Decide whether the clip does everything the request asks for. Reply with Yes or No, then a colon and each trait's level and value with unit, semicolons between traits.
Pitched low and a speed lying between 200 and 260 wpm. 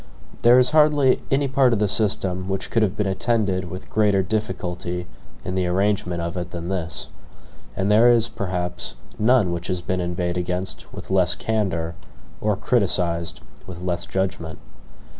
No: very low, 95 Hz; average, 160 wpm